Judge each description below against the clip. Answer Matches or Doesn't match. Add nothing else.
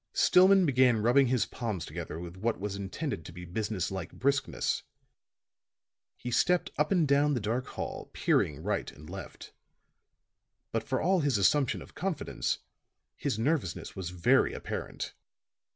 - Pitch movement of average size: Doesn't match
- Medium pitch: Doesn't match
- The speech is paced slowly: Doesn't match